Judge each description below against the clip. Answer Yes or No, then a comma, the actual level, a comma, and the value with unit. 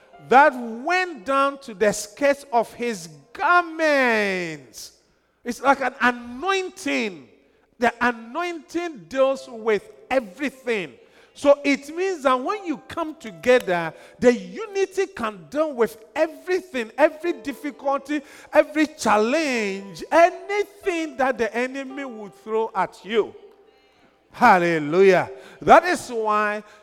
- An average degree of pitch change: No, wide, 6.4 semitones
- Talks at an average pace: No, slow, 105 wpm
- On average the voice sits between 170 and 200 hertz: No, very high, 265 Hz